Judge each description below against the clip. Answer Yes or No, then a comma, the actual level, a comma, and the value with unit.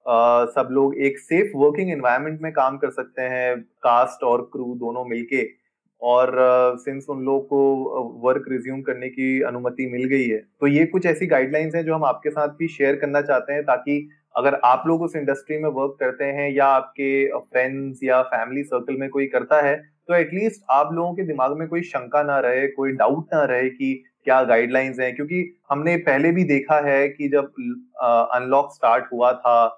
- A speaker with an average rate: No, fast, 200 wpm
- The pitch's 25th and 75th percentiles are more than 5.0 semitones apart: No, average, 2.8 semitones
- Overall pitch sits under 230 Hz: Yes, medium, 140 Hz